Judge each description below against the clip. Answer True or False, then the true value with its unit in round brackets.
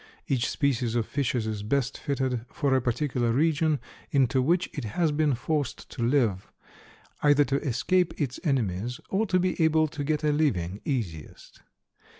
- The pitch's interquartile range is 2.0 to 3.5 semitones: False (4.2 semitones)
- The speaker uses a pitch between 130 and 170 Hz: True (135 Hz)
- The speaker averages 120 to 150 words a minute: False (160 wpm)